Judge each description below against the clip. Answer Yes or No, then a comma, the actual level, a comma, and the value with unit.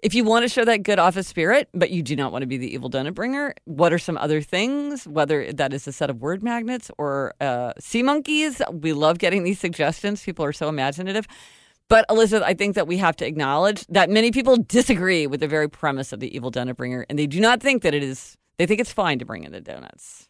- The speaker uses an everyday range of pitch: No, wide, 7.4 semitones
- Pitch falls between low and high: Yes, medium, 175 Hz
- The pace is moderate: No, fast, 250 wpm